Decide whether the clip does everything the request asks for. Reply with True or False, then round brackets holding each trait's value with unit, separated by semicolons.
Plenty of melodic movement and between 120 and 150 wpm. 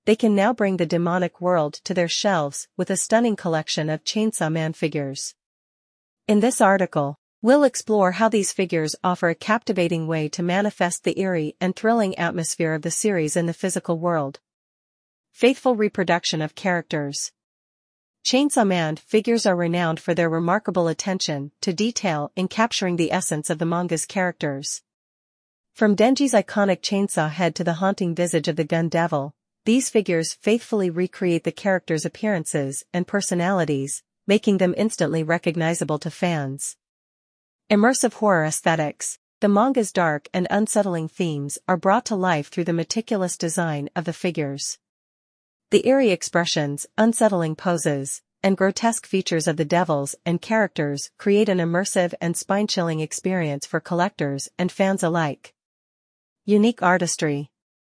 False (4.0 semitones; 145 wpm)